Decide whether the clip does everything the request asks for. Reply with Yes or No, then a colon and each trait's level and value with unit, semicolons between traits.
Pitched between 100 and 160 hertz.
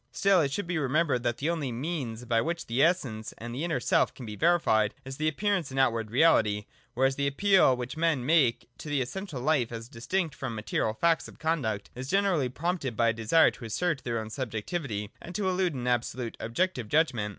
Yes: low, 135 Hz